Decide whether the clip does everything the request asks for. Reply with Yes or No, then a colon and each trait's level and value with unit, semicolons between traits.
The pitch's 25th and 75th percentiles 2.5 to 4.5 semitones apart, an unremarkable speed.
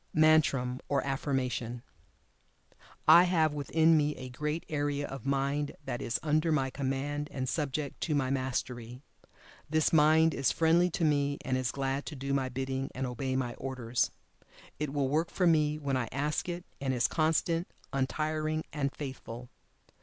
Yes: average, 2.8 semitones; average, 160 wpm